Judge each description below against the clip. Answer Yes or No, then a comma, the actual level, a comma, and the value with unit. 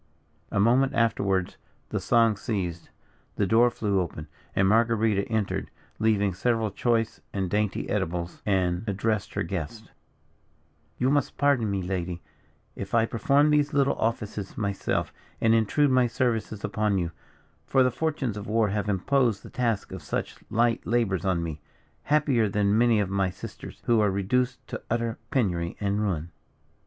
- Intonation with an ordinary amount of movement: Yes, average, 3.4 semitones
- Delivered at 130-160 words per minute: Yes, average, 155 wpm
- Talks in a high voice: No, low, 105 Hz